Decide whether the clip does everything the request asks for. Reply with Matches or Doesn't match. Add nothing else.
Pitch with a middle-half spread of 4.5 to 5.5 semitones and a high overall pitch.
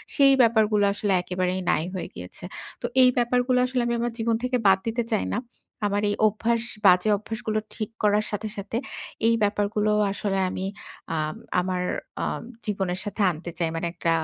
Doesn't match